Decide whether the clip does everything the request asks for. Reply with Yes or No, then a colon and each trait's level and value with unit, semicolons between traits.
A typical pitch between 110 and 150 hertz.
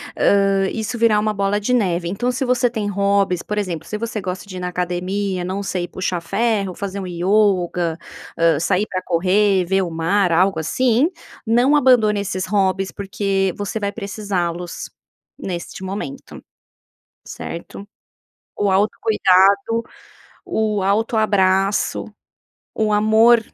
No: high, 200 Hz